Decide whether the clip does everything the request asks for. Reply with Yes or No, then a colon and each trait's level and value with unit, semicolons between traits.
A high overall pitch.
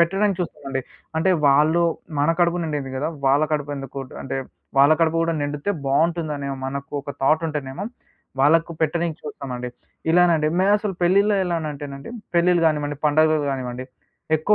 No: medium, 155 Hz